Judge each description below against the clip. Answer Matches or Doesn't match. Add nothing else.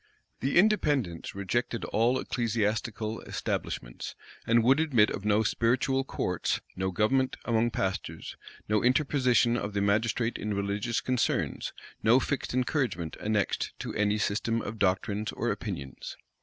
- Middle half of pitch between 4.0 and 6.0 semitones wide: Doesn't match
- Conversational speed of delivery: Doesn't match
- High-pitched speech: Doesn't match